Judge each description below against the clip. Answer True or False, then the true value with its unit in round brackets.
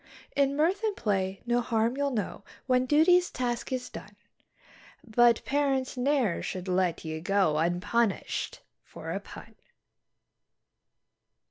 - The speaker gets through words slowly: True (125 wpm)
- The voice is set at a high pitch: True (240 Hz)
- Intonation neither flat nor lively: False (6.2 semitones)